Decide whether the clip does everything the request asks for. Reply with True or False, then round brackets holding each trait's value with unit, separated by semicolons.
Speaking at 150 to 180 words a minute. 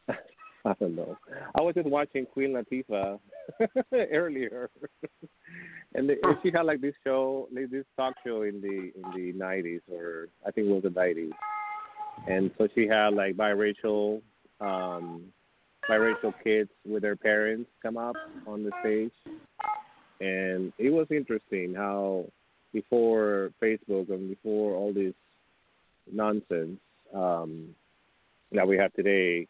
False (135 wpm)